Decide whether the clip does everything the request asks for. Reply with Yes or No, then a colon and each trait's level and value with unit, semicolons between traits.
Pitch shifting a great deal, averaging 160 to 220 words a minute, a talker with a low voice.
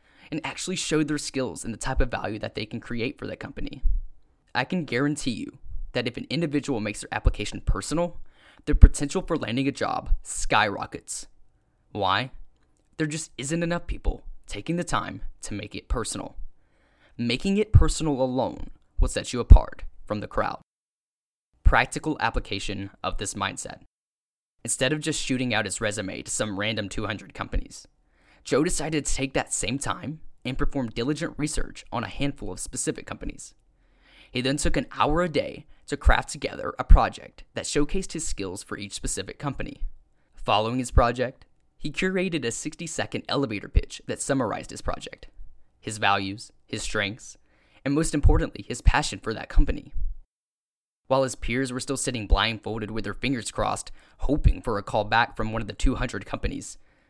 Yes: wide, 6.3 semitones; average, 170 wpm; low, 120 Hz